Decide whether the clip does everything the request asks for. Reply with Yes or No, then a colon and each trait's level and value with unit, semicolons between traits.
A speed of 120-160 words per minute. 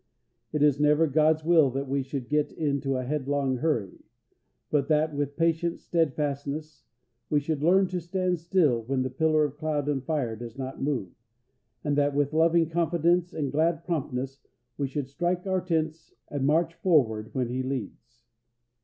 No: average, 170 wpm